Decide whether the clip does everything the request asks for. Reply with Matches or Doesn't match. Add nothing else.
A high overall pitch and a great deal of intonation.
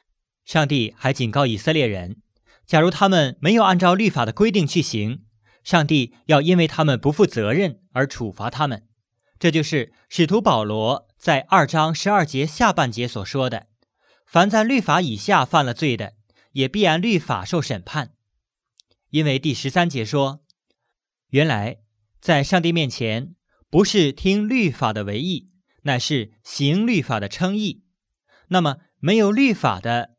Doesn't match